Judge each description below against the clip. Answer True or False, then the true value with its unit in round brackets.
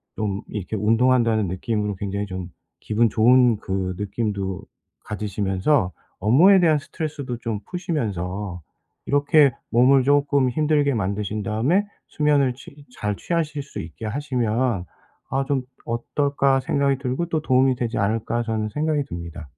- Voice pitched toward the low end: True (120 Hz)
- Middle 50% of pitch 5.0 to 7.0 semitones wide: True (5.4 semitones)